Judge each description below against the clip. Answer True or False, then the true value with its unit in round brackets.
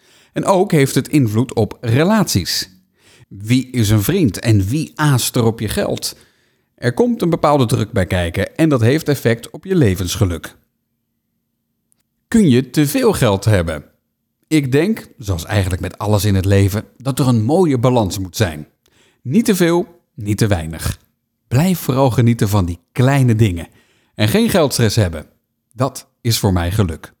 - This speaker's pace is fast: False (170 wpm)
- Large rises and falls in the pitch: True (6.1 semitones)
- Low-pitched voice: True (115 Hz)